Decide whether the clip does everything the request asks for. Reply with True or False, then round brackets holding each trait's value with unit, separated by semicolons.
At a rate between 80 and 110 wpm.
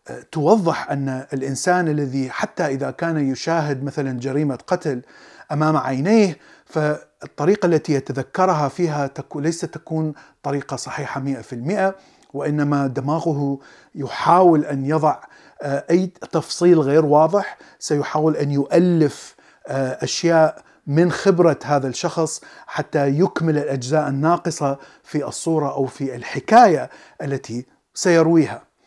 True (105 wpm)